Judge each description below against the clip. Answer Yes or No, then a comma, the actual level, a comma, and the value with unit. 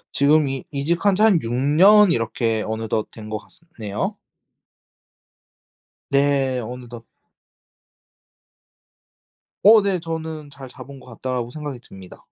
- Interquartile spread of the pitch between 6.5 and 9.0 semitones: No, wide, 5.4 semitones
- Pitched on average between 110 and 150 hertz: Yes, low, 135 Hz